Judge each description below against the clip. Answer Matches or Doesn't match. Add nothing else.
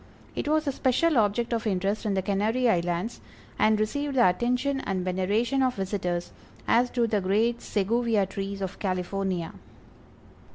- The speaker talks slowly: Doesn't match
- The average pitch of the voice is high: Matches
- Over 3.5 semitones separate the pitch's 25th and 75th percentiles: Matches